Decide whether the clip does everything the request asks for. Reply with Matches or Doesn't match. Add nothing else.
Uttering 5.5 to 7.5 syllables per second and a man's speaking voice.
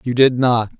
Doesn't match